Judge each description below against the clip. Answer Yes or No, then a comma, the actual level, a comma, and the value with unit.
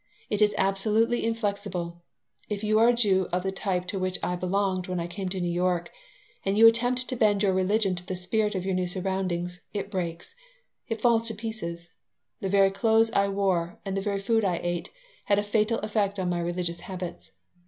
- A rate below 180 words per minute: No, fast, 205 wpm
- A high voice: Yes, high, 195 Hz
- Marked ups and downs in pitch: No, average, 3.0 semitones